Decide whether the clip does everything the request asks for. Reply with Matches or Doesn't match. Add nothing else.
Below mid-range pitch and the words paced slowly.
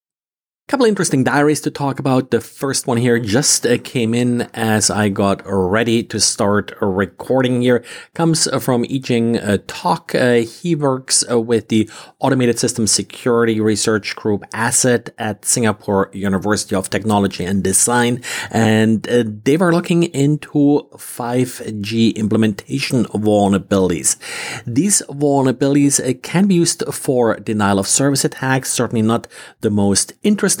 Matches